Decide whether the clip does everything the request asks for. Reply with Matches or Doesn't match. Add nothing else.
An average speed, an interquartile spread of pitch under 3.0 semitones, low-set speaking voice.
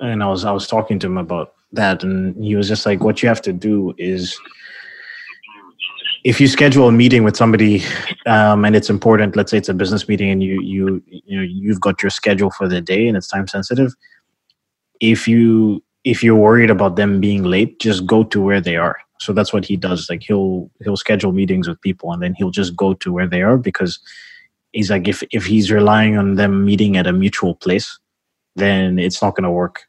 Doesn't match